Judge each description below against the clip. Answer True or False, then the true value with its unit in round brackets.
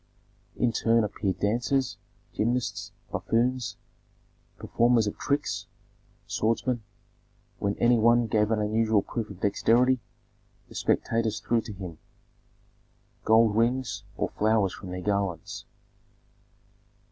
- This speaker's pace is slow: True (110 wpm)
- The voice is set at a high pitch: False (115 Hz)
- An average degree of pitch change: False (2.3 semitones)